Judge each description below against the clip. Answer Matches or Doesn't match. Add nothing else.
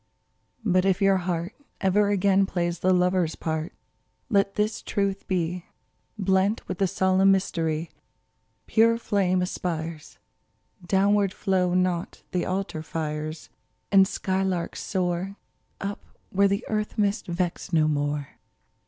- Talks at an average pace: Doesn't match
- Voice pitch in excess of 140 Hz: Matches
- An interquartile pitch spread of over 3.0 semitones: Doesn't match